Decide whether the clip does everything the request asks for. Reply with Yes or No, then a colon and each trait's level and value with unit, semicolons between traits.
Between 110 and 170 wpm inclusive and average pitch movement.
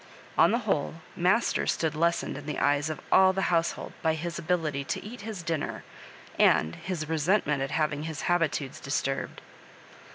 Yes: average, 165 wpm; average, 3.5 semitones